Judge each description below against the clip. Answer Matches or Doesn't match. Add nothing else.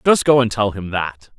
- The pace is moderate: Doesn't match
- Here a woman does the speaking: Doesn't match